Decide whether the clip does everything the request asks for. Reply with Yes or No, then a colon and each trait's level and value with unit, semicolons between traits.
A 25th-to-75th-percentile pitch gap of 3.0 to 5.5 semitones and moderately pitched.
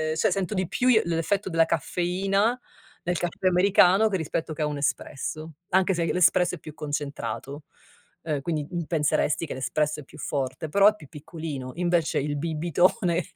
Yes: average, 3.3 semitones; medium, 165 Hz